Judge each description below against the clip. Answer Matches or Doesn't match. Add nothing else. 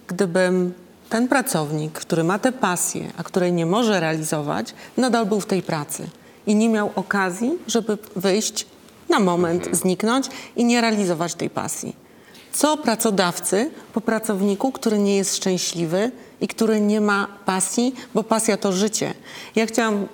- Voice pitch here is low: Doesn't match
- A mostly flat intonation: Doesn't match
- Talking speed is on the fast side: Doesn't match